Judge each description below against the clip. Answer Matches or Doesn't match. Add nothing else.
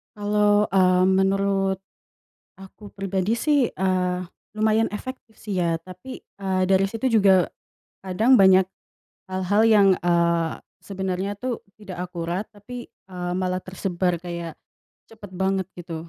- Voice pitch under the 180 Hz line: Doesn't match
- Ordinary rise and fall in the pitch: Doesn't match